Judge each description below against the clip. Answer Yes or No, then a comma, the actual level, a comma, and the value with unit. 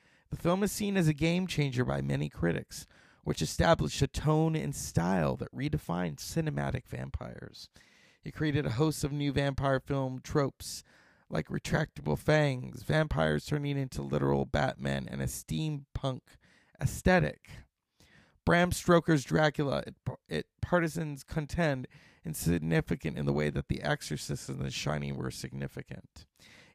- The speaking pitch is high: No, low, 135 Hz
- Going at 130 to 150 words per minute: Yes, slow, 135 wpm